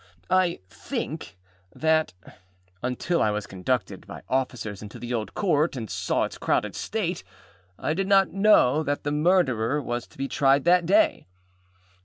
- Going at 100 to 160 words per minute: Yes, average, 155 wpm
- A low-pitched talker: No, medium, 145 Hz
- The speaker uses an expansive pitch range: Yes, wide, 6.6 semitones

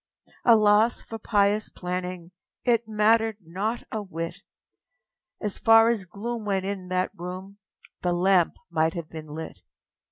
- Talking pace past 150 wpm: No, average, 140 wpm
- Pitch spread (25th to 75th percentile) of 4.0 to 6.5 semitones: No, average, 3.5 semitones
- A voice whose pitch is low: No, high, 200 Hz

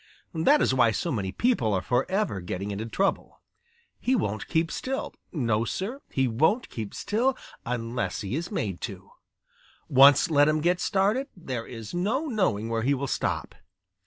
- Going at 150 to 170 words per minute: Yes, average, 165 wpm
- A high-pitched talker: No, medium, 140 Hz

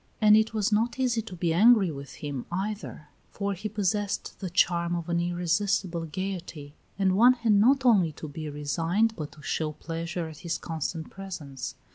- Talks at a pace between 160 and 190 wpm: Yes, average, 180 wpm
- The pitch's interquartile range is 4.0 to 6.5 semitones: Yes, average, 4.4 semitones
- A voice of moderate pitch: Yes, medium, 180 Hz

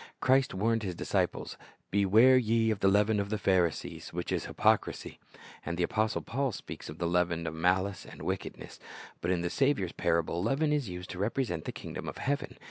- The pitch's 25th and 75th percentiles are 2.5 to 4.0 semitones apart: No, average, 4.6 semitones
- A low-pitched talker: Yes, low, 100 Hz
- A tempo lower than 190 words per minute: No, average, 195 wpm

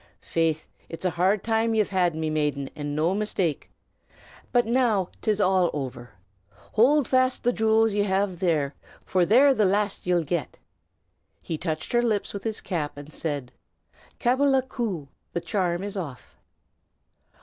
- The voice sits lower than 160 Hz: No, high, 190 Hz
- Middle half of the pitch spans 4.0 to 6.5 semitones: Yes, wide, 5.6 semitones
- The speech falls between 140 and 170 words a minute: Yes, average, 155 wpm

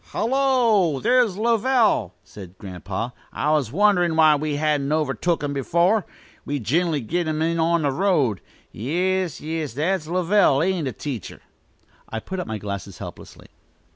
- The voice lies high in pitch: No, medium, 160 Hz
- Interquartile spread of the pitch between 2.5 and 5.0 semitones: No, wide, 5.4 semitones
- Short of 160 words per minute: Yes, average, 150 wpm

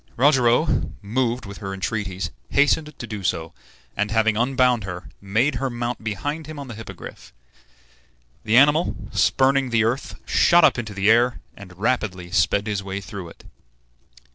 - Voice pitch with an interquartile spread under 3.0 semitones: No, average, 4.6 semitones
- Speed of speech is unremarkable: Yes, average, 160 wpm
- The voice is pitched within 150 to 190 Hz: No, low, 110 Hz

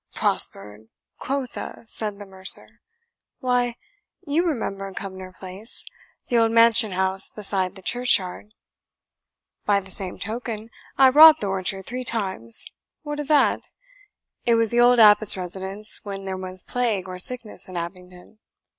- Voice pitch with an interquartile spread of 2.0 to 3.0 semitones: No, average, 4.2 semitones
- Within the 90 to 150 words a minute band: Yes, average, 140 wpm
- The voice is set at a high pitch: Yes, high, 205 Hz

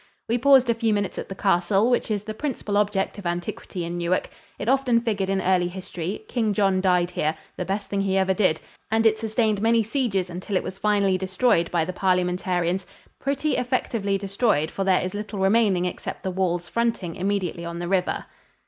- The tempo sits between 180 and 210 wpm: Yes, average, 200 wpm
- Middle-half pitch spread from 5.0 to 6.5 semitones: No, average, 3.3 semitones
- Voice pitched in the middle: No, high, 195 Hz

